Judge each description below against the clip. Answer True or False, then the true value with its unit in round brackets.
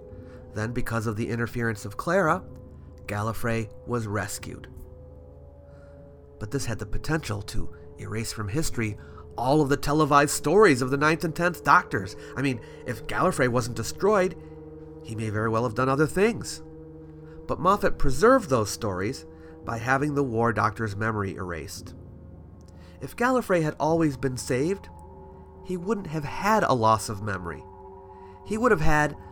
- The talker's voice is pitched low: True (115 Hz)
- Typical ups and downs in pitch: False (7.9 semitones)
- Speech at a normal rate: True (150 wpm)